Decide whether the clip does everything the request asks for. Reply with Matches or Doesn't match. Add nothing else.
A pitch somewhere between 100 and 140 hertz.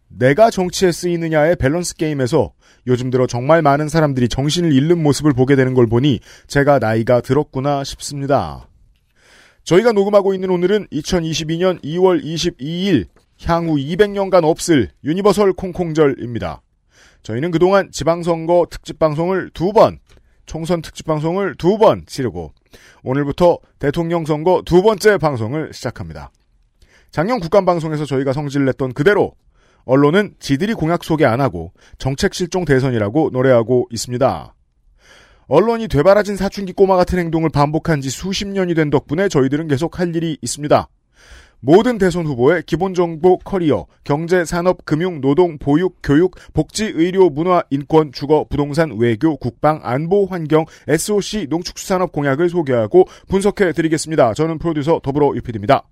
Doesn't match